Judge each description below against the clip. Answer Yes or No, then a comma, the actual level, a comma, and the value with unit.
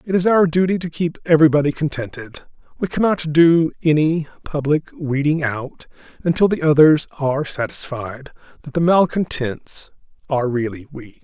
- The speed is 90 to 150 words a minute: Yes, average, 140 wpm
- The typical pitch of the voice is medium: Yes, medium, 150 Hz